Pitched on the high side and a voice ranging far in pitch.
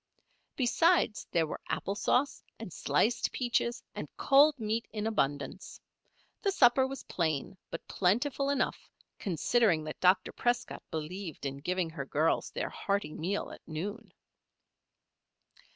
Yes: high, 200 Hz; wide, 7.0 semitones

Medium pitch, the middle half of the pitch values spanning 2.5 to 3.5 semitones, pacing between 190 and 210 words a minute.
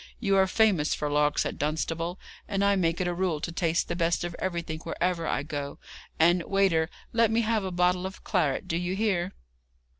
Yes: medium, 175 Hz; average, 2.8 semitones; fast, 205 wpm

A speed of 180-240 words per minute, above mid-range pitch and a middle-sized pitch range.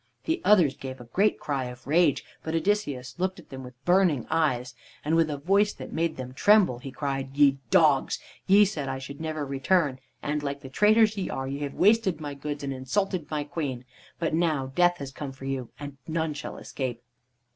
No: fast, 205 wpm; medium, 145 Hz; average, 4.7 semitones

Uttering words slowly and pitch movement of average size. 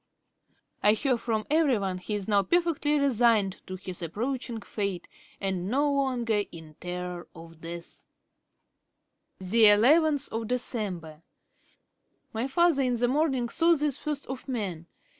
No: slow, 125 wpm; wide, 6.5 semitones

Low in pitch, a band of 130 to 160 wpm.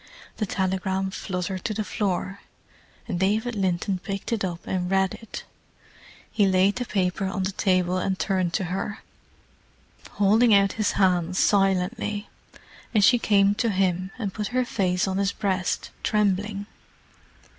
No: high, 195 Hz; average, 150 wpm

